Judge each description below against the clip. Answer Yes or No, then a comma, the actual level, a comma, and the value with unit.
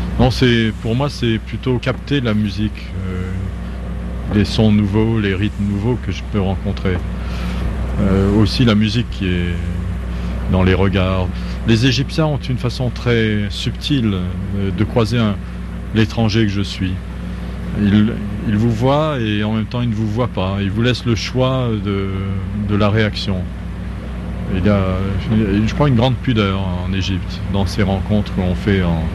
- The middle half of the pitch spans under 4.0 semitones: Yes, average, 3.4 semitones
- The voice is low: Yes, low, 100 Hz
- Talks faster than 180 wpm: No, average, 170 wpm